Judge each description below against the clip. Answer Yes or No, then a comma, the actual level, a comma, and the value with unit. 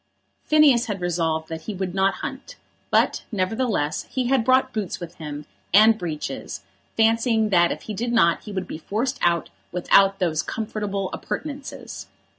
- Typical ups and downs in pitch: Yes, average, 4.8 semitones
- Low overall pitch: No, high, 200 Hz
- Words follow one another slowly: No, average, 160 wpm